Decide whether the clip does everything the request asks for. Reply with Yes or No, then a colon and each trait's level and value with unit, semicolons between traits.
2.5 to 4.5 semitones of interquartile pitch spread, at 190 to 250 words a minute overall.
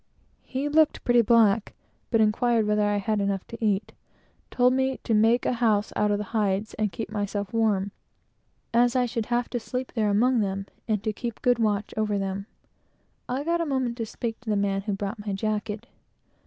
Yes: average, 2.8 semitones; average, 200 wpm